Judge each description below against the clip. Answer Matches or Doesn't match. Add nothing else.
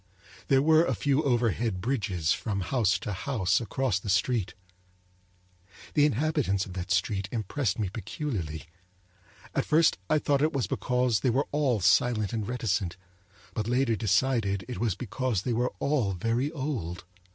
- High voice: Doesn't match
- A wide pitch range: Matches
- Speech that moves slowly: Doesn't match